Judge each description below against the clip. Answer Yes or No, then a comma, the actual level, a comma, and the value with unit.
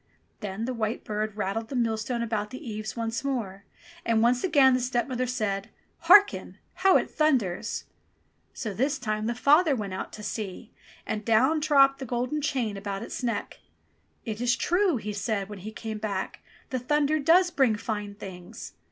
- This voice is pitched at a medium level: No, high, 230 Hz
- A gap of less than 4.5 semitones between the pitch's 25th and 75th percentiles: Yes, average, 3.9 semitones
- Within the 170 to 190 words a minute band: Yes, average, 180 wpm